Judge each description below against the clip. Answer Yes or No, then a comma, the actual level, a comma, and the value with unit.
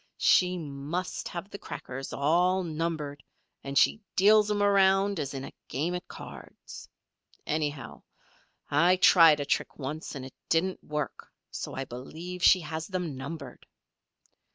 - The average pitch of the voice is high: No, medium, 165 Hz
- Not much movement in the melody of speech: No, average, 4.3 semitones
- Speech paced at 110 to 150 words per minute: Yes, average, 145 wpm